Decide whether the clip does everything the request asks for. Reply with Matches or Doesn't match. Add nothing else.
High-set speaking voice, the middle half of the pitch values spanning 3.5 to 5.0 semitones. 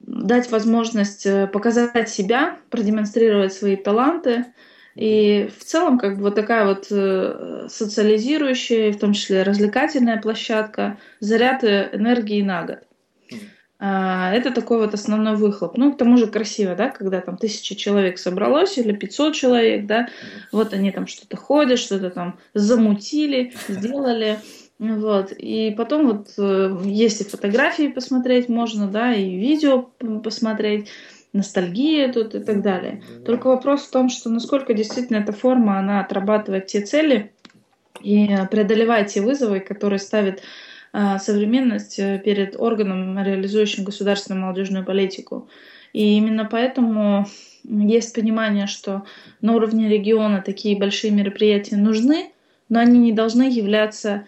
Doesn't match